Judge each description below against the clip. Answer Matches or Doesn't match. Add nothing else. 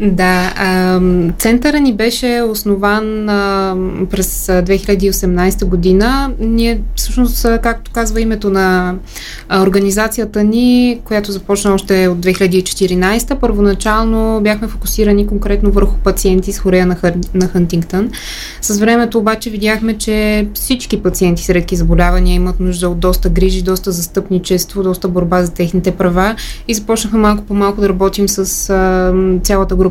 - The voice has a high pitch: Matches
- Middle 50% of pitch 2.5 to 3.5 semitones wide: Matches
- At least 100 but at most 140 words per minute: Matches